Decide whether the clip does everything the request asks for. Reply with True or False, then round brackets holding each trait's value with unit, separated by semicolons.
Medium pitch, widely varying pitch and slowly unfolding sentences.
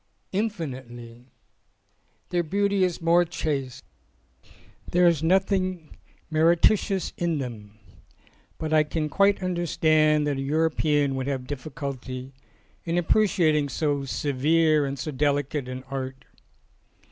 False (155 Hz; 4.2 semitones; 110 wpm)